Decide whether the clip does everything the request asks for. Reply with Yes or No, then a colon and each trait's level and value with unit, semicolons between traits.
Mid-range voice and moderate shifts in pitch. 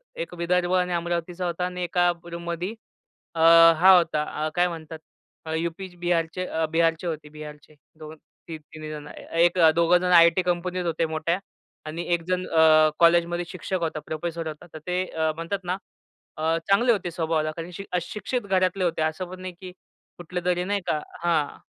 No: medium, 170 Hz; narrow, 2.0 semitones